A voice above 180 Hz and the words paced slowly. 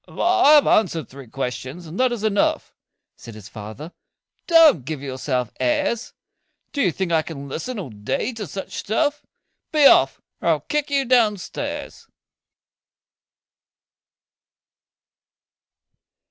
Yes: high, 190 Hz; slow, 130 wpm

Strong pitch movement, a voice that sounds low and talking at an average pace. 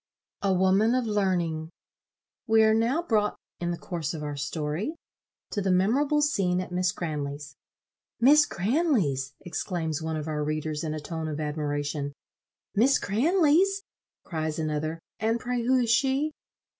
No: wide, 7.3 semitones; medium, 180 Hz; average, 150 wpm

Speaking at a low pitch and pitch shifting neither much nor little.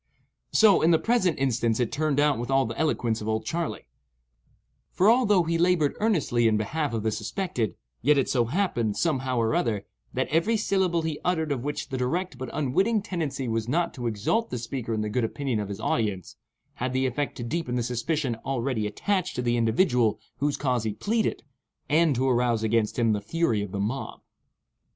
No: low, 130 Hz; wide, 6.2 semitones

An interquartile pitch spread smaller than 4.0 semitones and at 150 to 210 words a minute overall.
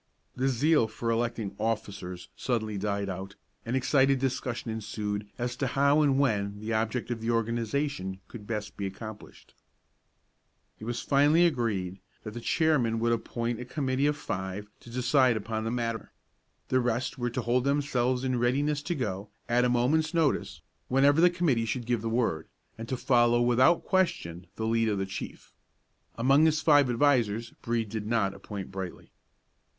Yes: average, 3.5 semitones; average, 170 wpm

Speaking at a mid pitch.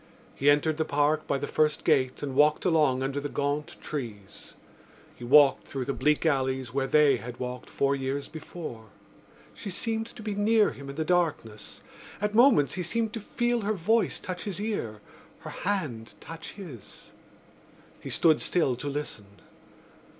Yes: medium, 150 Hz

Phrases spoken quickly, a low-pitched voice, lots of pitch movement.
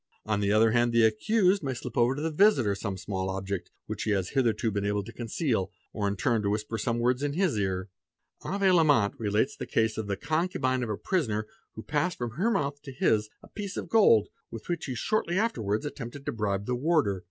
Yes: fast, 225 wpm; low, 115 Hz; wide, 6.1 semitones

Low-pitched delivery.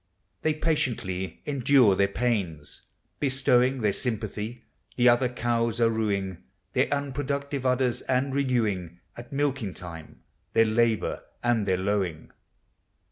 Yes: low, 120 Hz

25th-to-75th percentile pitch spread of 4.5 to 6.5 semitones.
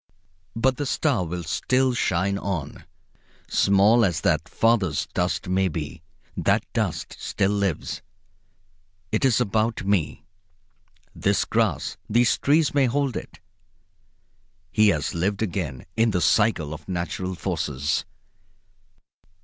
Yes: average, 5.2 semitones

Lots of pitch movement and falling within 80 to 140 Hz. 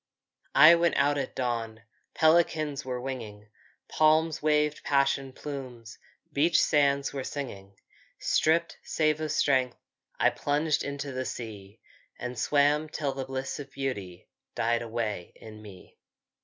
No: average, 4.2 semitones; low, 135 Hz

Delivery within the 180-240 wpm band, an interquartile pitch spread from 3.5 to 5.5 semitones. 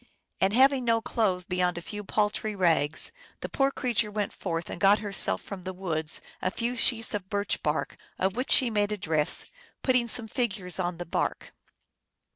Yes: average, 190 wpm; average, 4.0 semitones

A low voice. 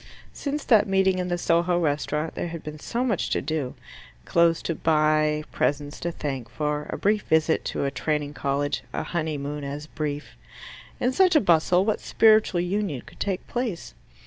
No: medium, 160 Hz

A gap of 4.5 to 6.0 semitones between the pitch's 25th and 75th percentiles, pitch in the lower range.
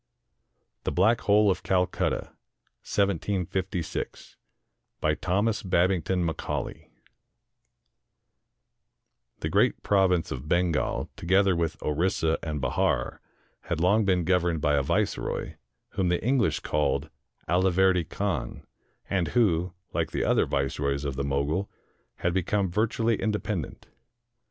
No: average, 3.5 semitones; very low, 90 Hz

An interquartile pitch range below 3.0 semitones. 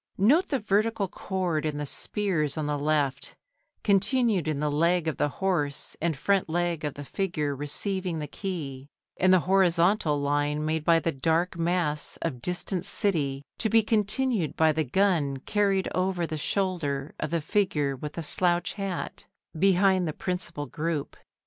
No: average, 4.4 semitones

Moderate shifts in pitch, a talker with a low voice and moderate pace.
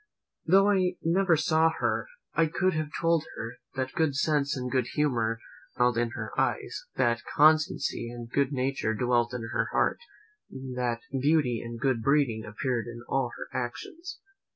Yes: average, 4.7 semitones; low, 130 Hz; average, 160 wpm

